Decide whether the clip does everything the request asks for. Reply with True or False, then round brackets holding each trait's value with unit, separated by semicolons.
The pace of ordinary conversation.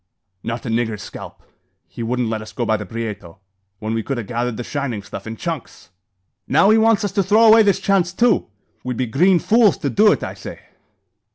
False (215 wpm)